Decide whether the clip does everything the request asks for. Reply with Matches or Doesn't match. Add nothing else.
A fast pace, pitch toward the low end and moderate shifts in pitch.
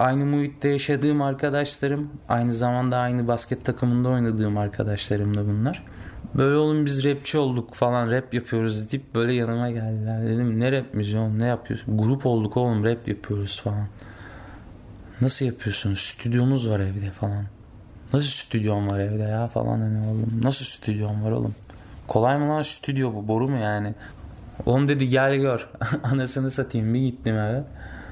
Matches